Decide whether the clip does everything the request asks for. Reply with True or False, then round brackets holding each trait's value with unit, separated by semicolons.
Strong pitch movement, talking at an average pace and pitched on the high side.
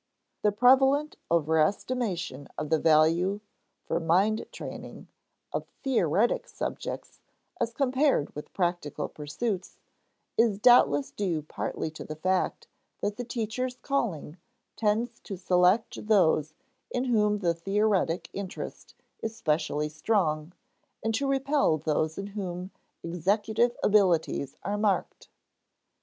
False (5.9 semitones; 115 wpm; 195 Hz)